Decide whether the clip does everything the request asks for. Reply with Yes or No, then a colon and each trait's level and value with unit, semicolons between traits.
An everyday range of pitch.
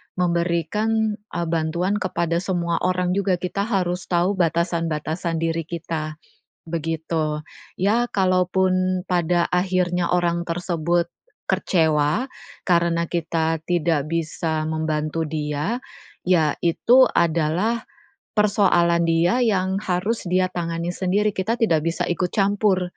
No: narrow, 2.1 semitones